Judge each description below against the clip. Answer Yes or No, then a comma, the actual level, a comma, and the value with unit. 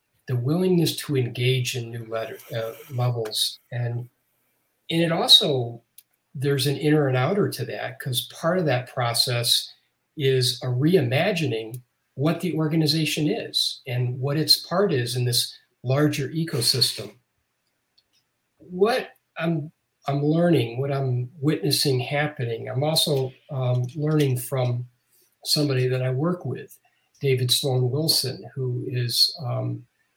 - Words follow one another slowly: Yes, slow, 130 wpm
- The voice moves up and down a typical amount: Yes, average, 3.3 semitones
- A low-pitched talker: Yes, low, 130 Hz